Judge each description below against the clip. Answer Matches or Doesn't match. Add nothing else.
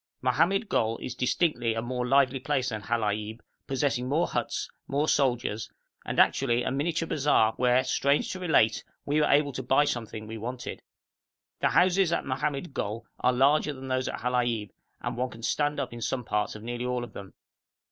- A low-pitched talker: Matches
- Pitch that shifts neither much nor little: Matches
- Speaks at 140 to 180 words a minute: Doesn't match